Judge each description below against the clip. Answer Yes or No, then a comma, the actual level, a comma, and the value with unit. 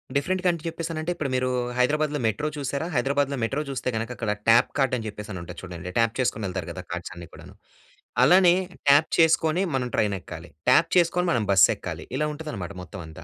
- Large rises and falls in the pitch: Yes, wide, 7.2 semitones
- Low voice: Yes, low, 130 Hz